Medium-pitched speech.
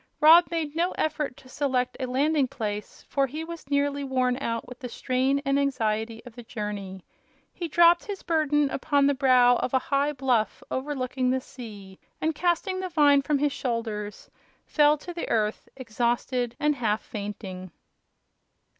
No: very high, 265 Hz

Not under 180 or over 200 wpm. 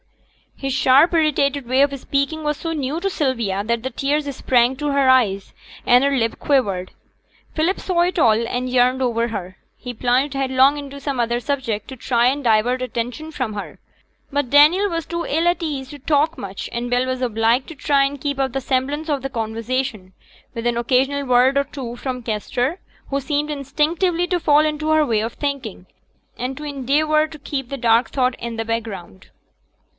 Yes: average, 190 wpm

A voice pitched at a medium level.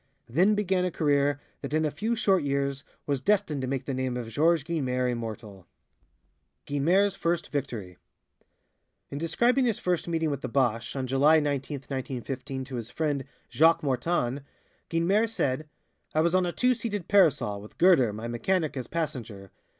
Yes: medium, 145 Hz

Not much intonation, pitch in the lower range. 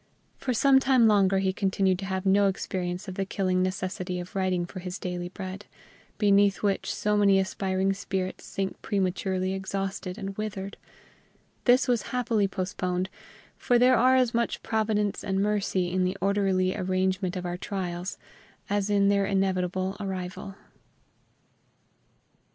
No: narrow, 1.7 semitones; high, 195 Hz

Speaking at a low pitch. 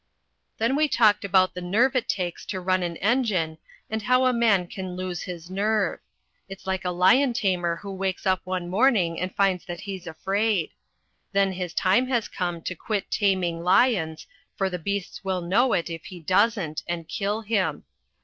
No: high, 190 Hz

